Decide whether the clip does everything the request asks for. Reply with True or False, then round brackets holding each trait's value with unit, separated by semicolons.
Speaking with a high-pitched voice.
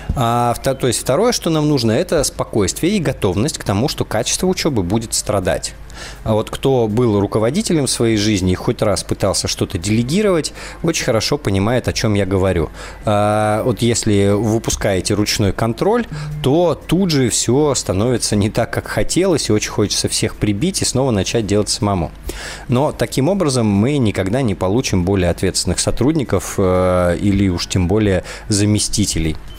False (110 Hz)